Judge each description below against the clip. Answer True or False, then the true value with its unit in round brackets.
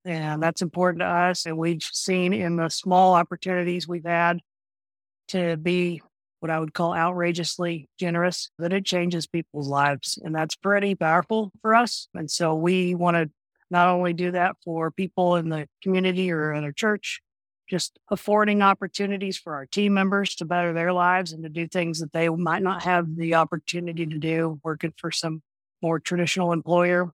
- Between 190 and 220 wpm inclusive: False (180 wpm)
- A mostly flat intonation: True (1.9 semitones)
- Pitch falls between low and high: True (175 Hz)